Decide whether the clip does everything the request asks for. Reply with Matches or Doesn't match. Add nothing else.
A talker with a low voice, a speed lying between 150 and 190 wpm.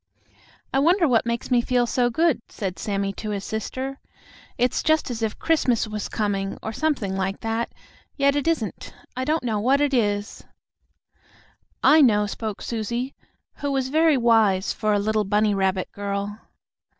Doesn't match